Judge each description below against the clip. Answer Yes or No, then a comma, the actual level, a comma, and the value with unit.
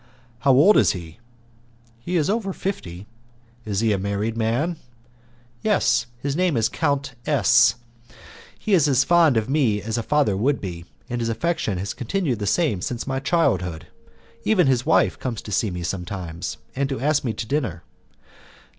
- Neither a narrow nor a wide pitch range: No, wide, 6.6 semitones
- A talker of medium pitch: No, low, 120 Hz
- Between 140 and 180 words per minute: Yes, average, 170 wpm